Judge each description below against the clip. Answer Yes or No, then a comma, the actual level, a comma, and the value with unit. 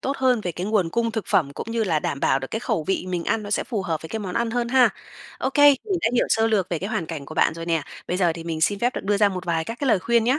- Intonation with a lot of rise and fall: Yes, wide, 5.8 semitones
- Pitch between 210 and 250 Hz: No, high, 200 Hz